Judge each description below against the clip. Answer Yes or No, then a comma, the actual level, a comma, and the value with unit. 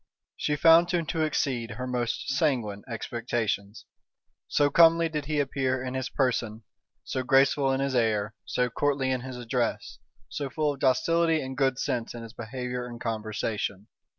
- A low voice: Yes, low, 130 Hz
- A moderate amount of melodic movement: Yes, average, 3.7 semitones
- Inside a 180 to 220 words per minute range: No, average, 165 wpm